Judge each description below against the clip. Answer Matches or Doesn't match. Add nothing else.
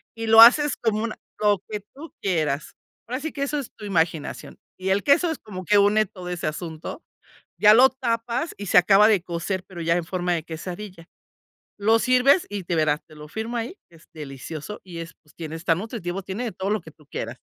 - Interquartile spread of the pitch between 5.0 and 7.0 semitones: Matches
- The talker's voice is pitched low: Doesn't match